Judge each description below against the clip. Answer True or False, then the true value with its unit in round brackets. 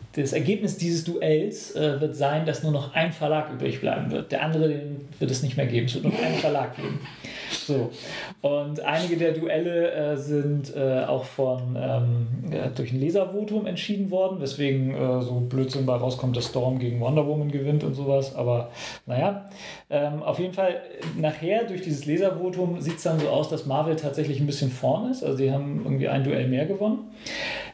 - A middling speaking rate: False (195 wpm)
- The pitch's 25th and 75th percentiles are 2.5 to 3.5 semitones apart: False (4.3 semitones)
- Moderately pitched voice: True (150 Hz)